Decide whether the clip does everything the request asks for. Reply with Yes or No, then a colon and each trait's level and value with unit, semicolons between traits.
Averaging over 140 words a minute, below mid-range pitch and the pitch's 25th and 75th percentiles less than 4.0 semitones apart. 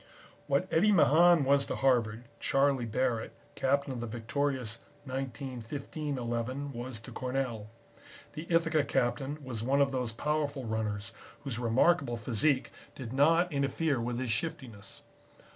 No: slow, 135 wpm; low, 130 Hz; average, 3.3 semitones